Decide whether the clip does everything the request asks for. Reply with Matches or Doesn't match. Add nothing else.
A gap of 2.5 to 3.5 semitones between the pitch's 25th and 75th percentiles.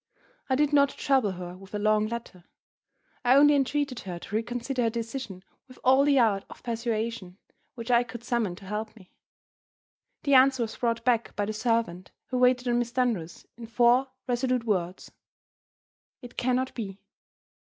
Matches